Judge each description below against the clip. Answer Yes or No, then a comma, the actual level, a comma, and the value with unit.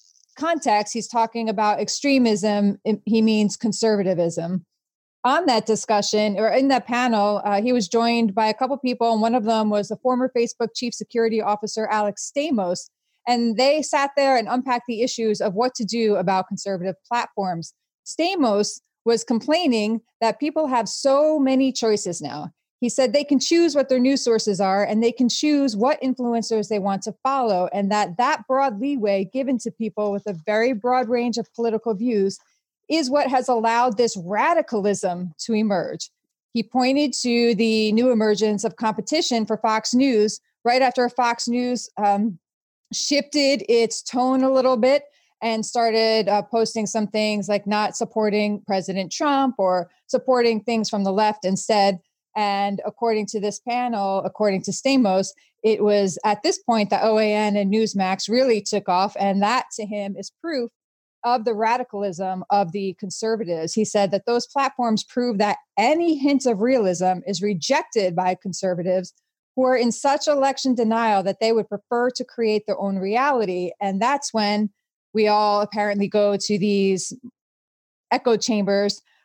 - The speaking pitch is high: Yes, high, 225 Hz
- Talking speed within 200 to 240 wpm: No, average, 165 wpm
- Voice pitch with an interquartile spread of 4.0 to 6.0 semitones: No, average, 3.3 semitones